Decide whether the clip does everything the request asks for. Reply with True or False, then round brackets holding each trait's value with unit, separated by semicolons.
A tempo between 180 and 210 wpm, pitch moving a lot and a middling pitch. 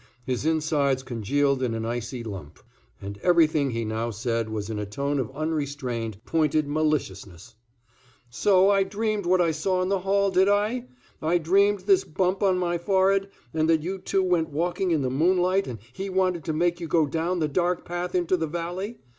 True (190 wpm; 5.7 semitones; 160 Hz)